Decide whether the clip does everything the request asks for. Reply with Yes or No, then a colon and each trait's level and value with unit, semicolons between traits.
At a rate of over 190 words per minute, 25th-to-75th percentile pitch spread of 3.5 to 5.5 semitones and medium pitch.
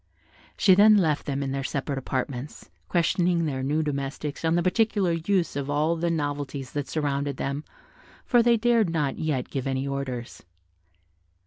No: average, 160 wpm; average, 3.8 semitones; medium, 150 Hz